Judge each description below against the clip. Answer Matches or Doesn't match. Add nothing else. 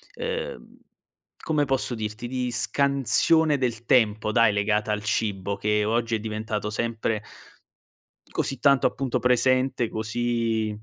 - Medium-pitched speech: Doesn't match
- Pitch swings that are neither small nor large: Matches